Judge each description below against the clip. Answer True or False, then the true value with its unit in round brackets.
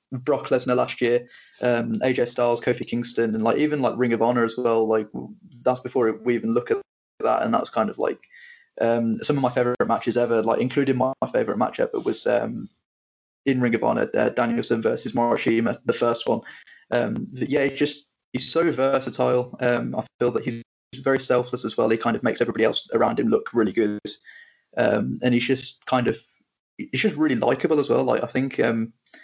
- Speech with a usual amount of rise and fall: False (2.2 semitones)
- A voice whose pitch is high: False (120 Hz)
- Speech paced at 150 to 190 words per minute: False (205 wpm)